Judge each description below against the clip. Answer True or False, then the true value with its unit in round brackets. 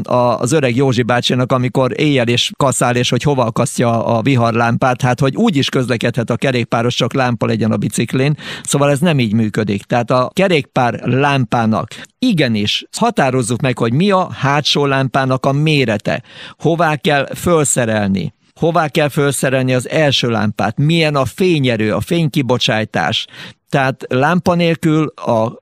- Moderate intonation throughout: True (3.6 semitones)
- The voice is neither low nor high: False (130 Hz)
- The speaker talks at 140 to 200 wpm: True (150 wpm)